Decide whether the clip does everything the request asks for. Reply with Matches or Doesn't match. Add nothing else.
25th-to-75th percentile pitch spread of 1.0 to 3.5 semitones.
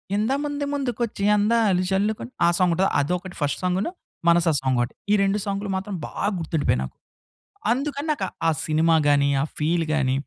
Doesn't match